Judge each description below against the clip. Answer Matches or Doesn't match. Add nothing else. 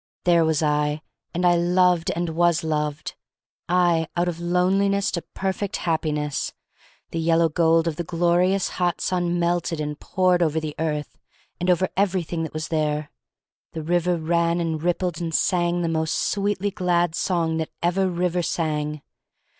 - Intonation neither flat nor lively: Doesn't match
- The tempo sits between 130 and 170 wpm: Matches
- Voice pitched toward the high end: Doesn't match